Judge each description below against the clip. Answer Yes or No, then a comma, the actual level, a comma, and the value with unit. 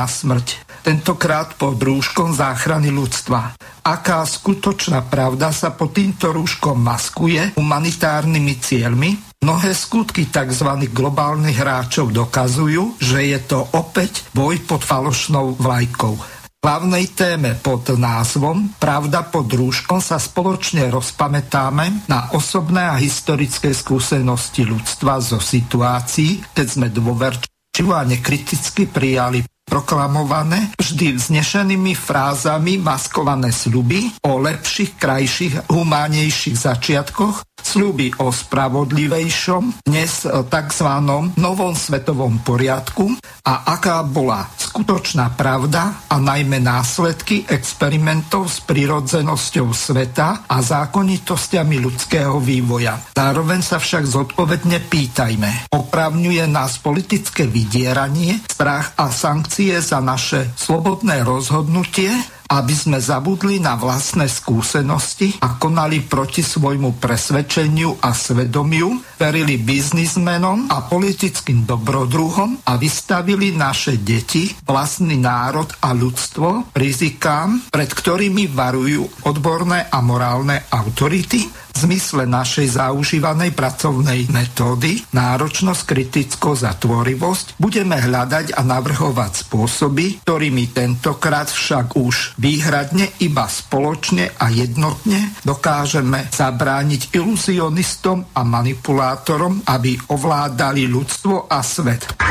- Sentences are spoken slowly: Yes, slow, 105 wpm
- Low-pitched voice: No, medium, 145 Hz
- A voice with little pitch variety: No, average, 4.4 semitones